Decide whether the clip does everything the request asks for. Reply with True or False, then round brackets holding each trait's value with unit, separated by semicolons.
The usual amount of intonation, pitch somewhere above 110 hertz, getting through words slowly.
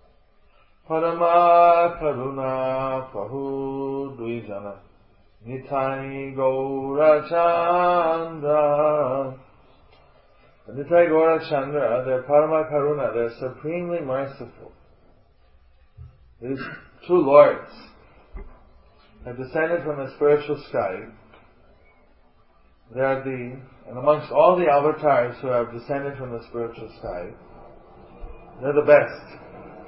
True (3.6 semitones; 135 Hz; 80 wpm)